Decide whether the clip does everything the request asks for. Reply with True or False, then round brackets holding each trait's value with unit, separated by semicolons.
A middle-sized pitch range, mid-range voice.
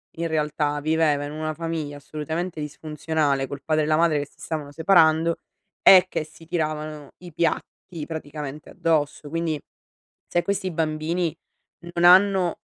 False (1.8 semitones; 155 Hz)